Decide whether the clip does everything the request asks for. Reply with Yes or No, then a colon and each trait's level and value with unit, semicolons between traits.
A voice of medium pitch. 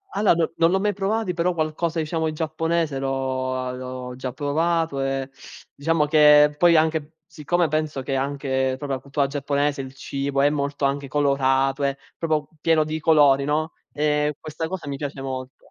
Yes: medium, 145 Hz